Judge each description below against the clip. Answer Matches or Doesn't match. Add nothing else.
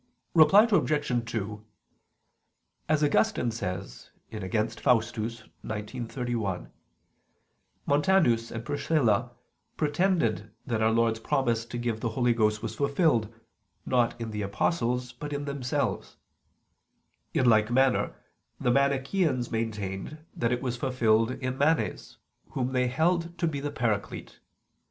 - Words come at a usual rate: Doesn't match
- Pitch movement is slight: Doesn't match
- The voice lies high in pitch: Doesn't match